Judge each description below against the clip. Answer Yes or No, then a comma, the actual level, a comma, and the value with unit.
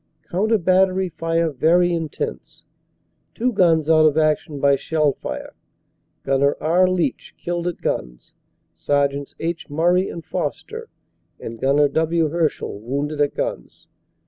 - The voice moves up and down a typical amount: Yes, average, 3.4 semitones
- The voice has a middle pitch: Yes, medium, 160 Hz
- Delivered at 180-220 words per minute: No, slow, 135 wpm